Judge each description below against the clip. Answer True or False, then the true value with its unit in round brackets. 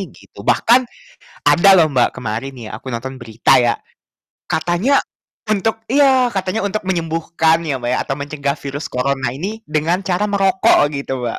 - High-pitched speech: False (160 Hz)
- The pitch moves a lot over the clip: True (6.3 semitones)